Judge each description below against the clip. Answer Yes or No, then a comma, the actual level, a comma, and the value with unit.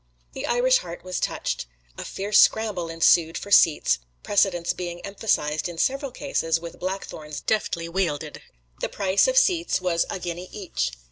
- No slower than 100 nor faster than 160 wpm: Yes, average, 155 wpm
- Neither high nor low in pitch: Yes, medium, 180 Hz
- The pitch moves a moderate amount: Yes, average, 3.8 semitones